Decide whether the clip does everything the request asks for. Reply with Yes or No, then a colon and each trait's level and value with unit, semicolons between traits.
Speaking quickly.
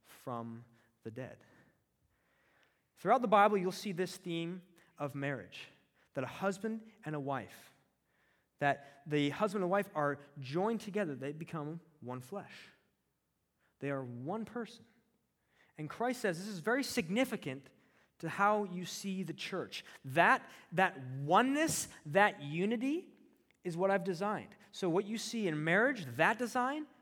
No: average, 140 wpm